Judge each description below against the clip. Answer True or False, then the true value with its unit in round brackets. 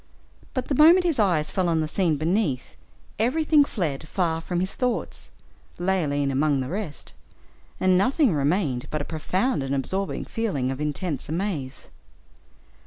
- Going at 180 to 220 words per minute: False (150 wpm)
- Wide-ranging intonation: True (6.0 semitones)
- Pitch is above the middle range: False (175 Hz)